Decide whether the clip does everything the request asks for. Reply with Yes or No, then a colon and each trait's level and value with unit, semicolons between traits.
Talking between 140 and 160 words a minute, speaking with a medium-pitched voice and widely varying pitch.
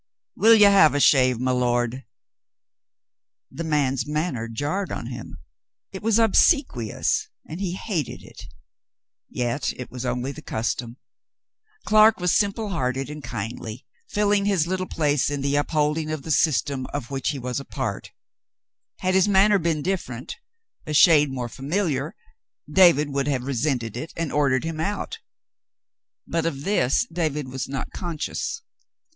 Yes: average, 155 wpm; medium, 150 Hz; wide, 5.7 semitones